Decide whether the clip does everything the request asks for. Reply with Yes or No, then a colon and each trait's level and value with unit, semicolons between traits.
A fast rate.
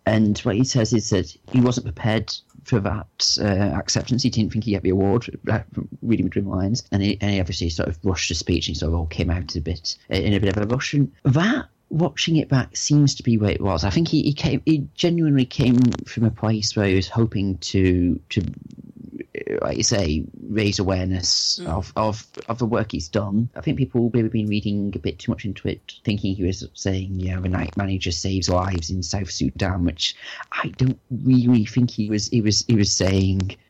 Yes: fast, 220 wpm